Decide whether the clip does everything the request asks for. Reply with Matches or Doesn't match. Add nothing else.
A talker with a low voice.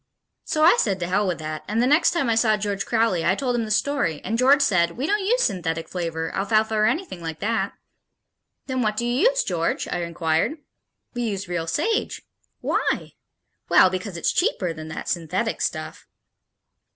Doesn't match